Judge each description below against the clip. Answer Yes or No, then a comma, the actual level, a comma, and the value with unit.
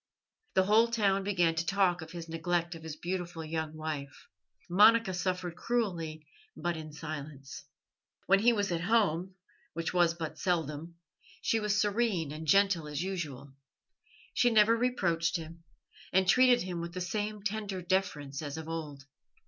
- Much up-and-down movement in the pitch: No, average, 3.7 semitones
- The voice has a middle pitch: Yes, medium, 175 Hz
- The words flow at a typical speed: Yes, average, 155 wpm